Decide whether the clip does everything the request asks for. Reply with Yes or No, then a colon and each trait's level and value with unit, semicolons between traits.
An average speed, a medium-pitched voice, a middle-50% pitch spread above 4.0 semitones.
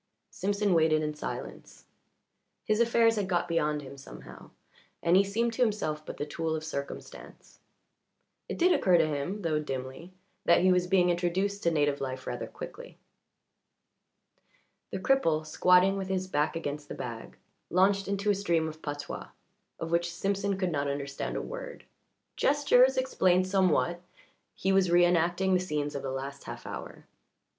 Yes: average, 160 wpm; medium, 175 Hz; average, 4.4 semitones